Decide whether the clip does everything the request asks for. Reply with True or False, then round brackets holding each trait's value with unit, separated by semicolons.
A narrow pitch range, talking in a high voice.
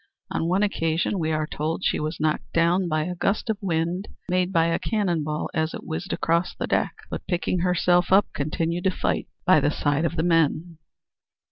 False (2.3 semitones; 170 Hz)